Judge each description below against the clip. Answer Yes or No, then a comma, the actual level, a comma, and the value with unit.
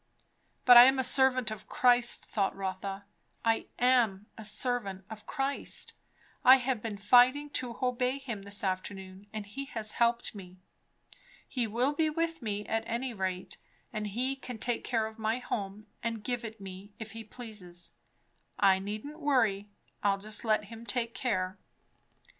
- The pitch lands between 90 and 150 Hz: No, high, 225 Hz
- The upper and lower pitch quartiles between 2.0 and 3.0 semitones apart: No, average, 3.7 semitones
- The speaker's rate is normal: Yes, average, 165 wpm